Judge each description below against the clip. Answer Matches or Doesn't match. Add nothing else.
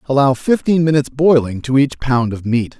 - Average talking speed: Matches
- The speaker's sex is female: Doesn't match